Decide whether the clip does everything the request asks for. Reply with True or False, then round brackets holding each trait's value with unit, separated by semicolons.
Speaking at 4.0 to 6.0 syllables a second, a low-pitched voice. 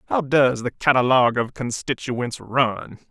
True (4.3 syllables/s; 130 Hz)